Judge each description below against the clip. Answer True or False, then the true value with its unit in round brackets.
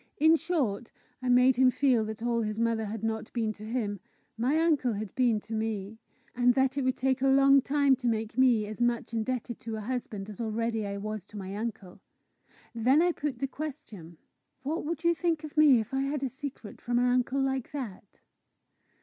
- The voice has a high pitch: True (245 Hz)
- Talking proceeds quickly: True (210 wpm)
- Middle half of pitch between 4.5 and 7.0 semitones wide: False (3.7 semitones)